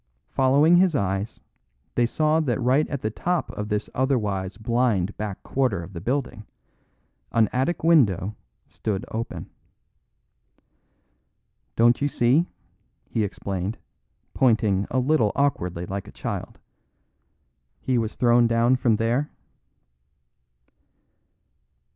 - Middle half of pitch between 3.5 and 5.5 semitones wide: Yes, average, 4.4 semitones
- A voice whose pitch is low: Yes, low, 120 Hz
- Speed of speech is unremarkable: No, slow, 115 wpm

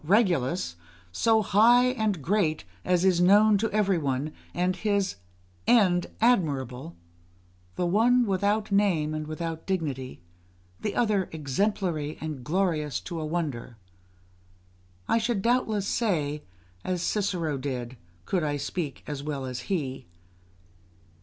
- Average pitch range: No, wide, 5.7 semitones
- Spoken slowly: Yes, slow, 125 wpm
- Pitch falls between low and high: Yes, medium, 175 Hz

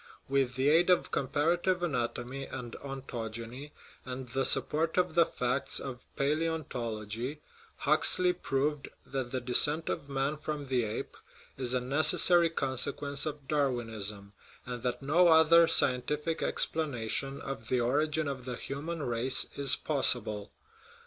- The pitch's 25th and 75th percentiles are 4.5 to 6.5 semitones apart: No, average, 3.6 semitones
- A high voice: No, low, 135 Hz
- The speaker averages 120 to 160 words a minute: Yes, average, 140 wpm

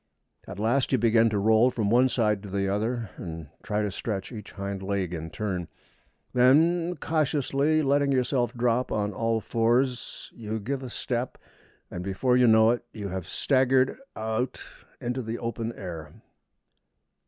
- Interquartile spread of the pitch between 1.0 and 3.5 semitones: No, average, 4.0 semitones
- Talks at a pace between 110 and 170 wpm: Yes, average, 160 wpm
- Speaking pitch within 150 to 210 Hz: No, low, 115 Hz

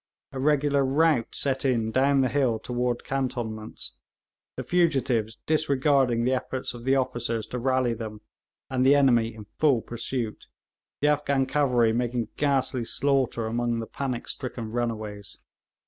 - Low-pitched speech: Yes, low, 125 Hz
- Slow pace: No, average, 145 wpm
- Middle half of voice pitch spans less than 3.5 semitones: Yes, average, 2.9 semitones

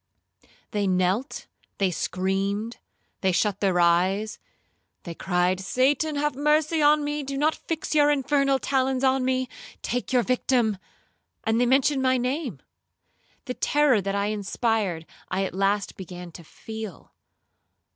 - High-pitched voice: Yes, high, 230 Hz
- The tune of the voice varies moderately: No, wide, 6.0 semitones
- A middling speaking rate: No, slow, 125 wpm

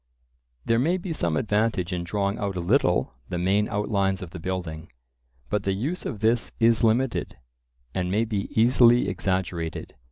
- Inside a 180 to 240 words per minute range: No, average, 165 wpm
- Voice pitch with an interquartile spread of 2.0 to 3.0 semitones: No, average, 4.0 semitones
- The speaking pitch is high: No, low, 100 Hz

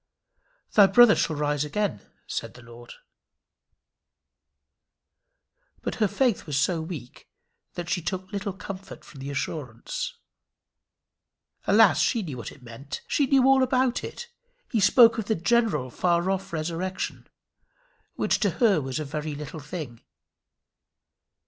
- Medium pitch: Yes, medium, 175 Hz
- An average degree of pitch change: No, wide, 6.4 semitones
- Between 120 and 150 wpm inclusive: Yes, slow, 135 wpm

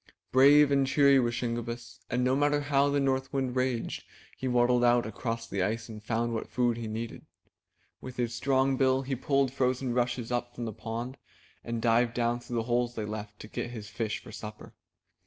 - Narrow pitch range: Yes, narrow, 2.2 semitones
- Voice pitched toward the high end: No, low, 120 Hz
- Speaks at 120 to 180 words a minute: No, average, 200 wpm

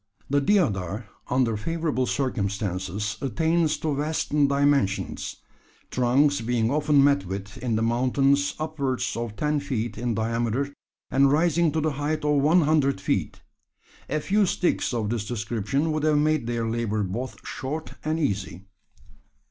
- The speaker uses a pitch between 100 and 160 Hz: Yes, low, 135 Hz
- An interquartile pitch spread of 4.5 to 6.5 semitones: Yes, average, 5.0 semitones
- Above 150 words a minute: No, average, 145 wpm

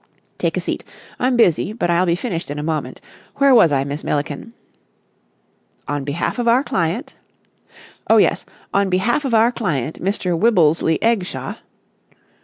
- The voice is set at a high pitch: No, medium, 180 Hz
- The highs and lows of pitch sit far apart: Yes, wide, 6.8 semitones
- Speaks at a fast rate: No, average, 155 wpm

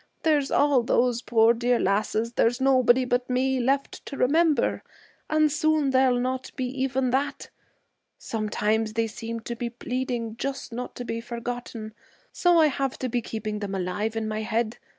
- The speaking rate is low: No, average, 170 wpm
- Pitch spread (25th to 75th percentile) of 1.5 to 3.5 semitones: Yes, average, 2.8 semitones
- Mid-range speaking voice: No, high, 245 Hz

